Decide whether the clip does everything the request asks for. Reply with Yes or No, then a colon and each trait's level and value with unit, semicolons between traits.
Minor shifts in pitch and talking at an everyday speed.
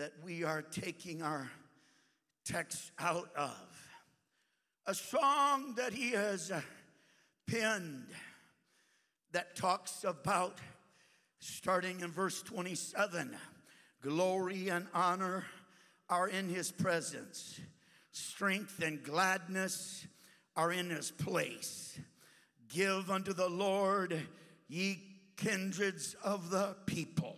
No: narrow, 2.1 semitones; slow, 95 wpm